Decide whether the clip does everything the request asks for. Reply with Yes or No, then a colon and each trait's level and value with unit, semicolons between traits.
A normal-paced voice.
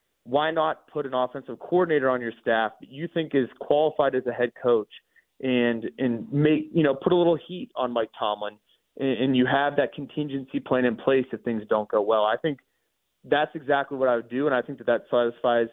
No: fast, 220 wpm